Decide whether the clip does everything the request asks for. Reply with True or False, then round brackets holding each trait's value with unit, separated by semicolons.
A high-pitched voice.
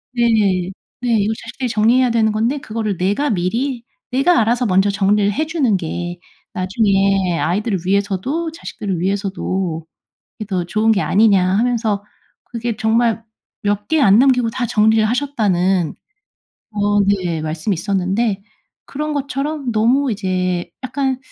True (215 Hz)